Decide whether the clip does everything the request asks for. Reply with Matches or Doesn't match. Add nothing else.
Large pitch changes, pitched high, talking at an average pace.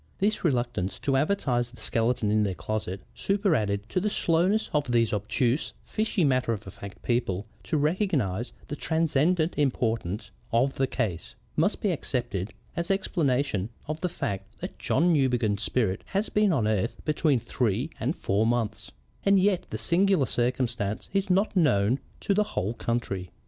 Doesn't match